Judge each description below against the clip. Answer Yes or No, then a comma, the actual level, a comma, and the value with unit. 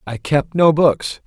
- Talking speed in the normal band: Yes, average, 190 wpm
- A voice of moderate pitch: Yes, medium, 150 Hz